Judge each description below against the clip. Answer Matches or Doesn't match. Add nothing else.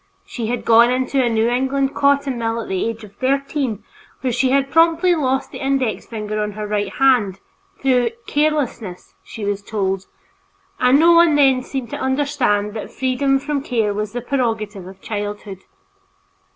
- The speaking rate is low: Doesn't match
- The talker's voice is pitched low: Doesn't match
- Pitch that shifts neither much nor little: Matches